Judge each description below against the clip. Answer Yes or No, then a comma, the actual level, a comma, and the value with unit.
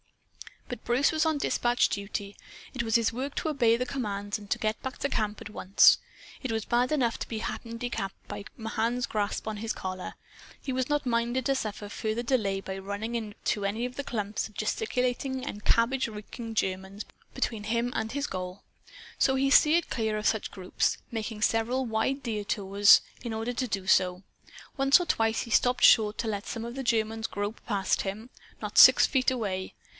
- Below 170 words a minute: No, average, 190 wpm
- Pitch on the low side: No, high, 225 Hz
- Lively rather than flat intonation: No, average, 3.3 semitones